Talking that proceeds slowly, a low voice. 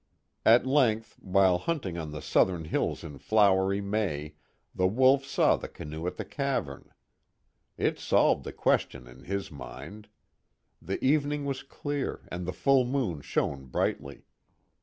No: average, 145 wpm; low, 100 Hz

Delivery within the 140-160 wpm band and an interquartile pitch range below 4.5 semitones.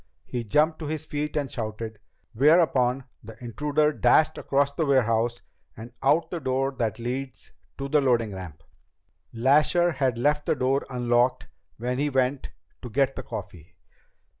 Yes: average, 155 wpm; average, 3.8 semitones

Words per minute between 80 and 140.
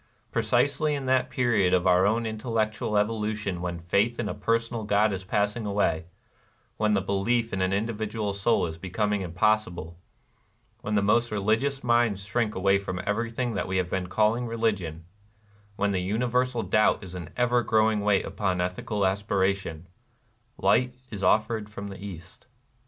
No: average, 170 wpm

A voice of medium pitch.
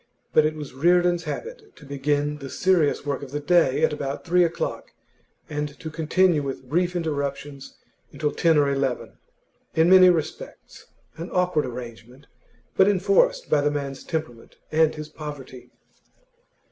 Yes: medium, 150 Hz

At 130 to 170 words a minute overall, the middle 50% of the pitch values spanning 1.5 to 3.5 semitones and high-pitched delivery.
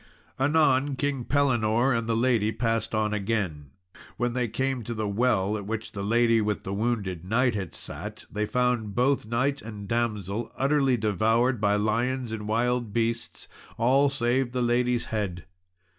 No: average, 165 wpm; average, 2.8 semitones; low, 115 Hz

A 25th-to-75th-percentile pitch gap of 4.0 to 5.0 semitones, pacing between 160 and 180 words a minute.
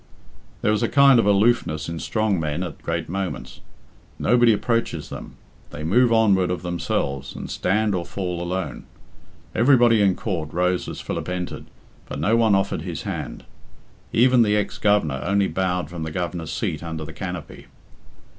Yes: average, 4.5 semitones; average, 165 wpm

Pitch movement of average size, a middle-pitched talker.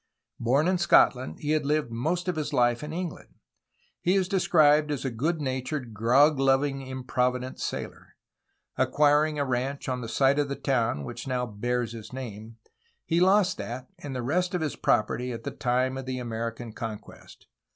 No: average, 3.8 semitones; low, 130 Hz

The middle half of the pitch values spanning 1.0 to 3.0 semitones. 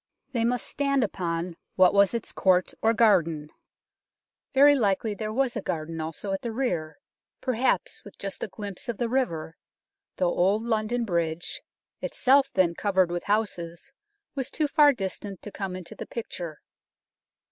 No: wide, 5.4 semitones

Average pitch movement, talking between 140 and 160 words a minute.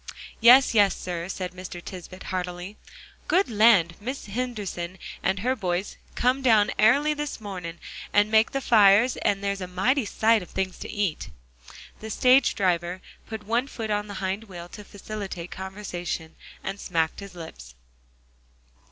Yes: average, 3.7 semitones; average, 155 wpm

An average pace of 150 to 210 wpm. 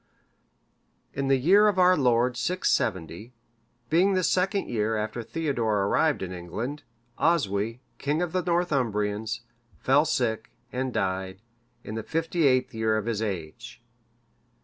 No: average, 140 wpm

